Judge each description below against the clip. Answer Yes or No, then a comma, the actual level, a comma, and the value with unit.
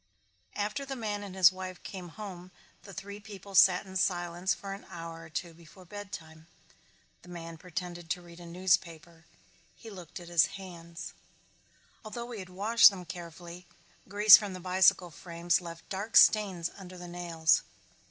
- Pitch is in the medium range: Yes, medium, 180 Hz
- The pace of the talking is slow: No, average, 165 wpm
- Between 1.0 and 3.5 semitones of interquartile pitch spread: Yes, narrow, 2.5 semitones